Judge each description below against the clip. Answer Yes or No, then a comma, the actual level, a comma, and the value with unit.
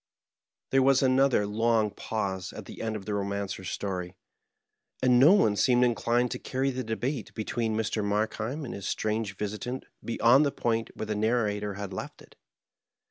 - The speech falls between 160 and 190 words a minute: Yes, average, 175 wpm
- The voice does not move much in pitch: No, average, 3.4 semitones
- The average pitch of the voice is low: Yes, low, 110 Hz